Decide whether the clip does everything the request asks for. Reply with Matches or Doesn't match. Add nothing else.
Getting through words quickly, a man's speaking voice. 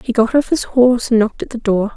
Doesn't match